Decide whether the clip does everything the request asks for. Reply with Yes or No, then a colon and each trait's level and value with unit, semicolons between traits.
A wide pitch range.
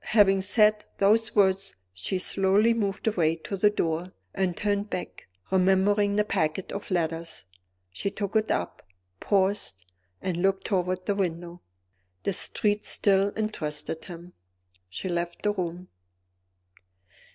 No: average, 2.8 semitones